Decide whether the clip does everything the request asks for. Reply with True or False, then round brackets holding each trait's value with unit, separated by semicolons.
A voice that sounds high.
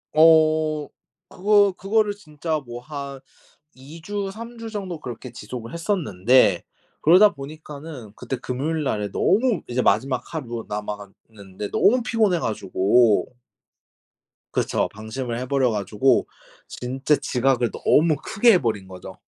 False (140 Hz)